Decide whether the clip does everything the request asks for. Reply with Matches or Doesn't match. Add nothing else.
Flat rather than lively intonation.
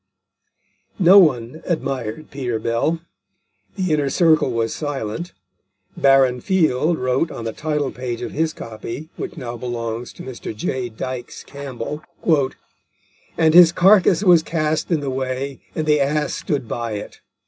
Doesn't match